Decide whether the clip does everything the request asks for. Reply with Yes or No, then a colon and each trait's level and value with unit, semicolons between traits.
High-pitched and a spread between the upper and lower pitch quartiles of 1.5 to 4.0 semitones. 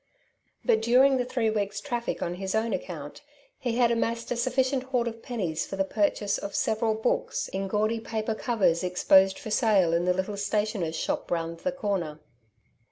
Yes: high, 215 Hz; average, 3.7 semitones